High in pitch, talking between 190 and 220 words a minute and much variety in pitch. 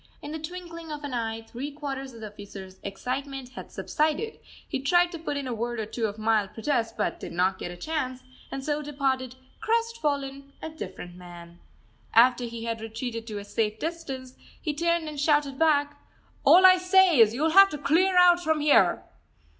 Yes: very high, 275 Hz; average, 195 wpm; wide, 5.8 semitones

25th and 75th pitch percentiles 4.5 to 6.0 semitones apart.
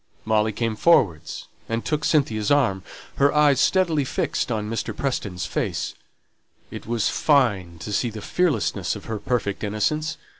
Yes: average, 5.3 semitones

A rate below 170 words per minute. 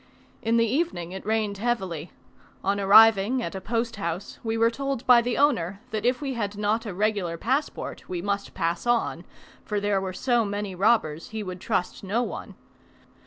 No: average, 180 wpm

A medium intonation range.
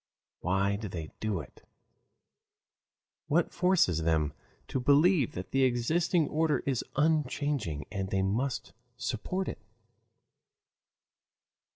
No: wide, 8.3 semitones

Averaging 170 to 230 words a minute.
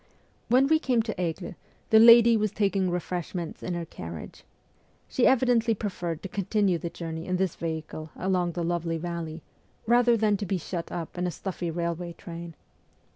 Yes: average, 175 wpm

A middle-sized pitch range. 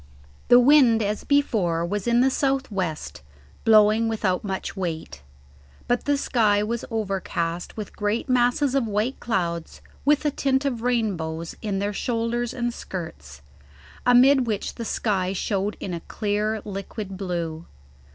Yes: average, 4.4 semitones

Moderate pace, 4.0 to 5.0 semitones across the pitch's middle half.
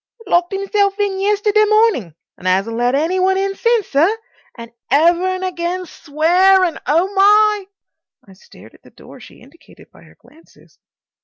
Yes: average, 160 wpm; average, 4.3 semitones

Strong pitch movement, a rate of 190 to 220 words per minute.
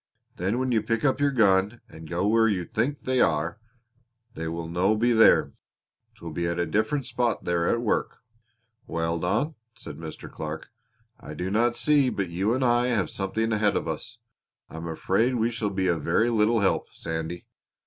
Yes: wide, 5.7 semitones; average, 195 wpm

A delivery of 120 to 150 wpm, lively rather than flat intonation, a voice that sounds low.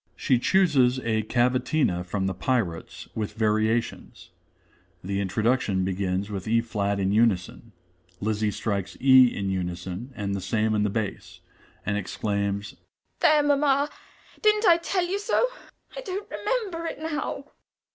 Yes: average, 140 wpm; wide, 8.1 semitones; low, 110 Hz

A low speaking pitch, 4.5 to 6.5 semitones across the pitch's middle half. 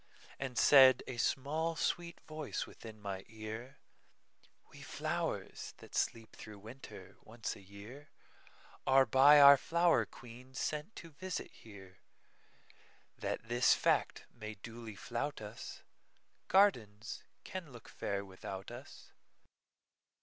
Yes: low, 120 Hz; average, 4.9 semitones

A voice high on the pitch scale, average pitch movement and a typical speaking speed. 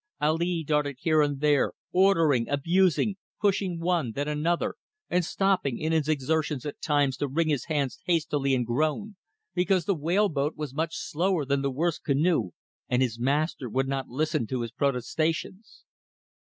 No: medium, 150 Hz; average, 3.6 semitones; average, 165 wpm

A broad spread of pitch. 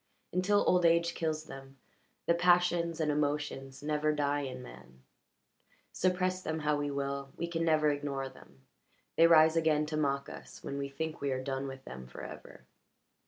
No: average, 3.2 semitones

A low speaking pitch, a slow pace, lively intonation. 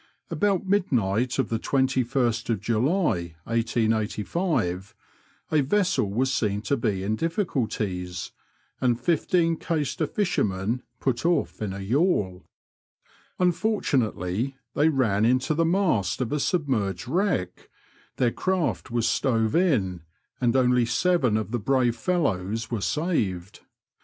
Yes: low, 120 Hz; slow, 120 wpm; wide, 7.1 semitones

